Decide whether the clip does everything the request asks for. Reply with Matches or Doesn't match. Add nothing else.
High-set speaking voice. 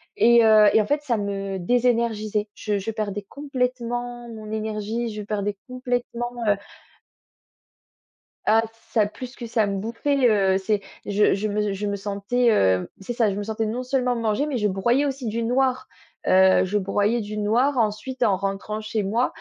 Matches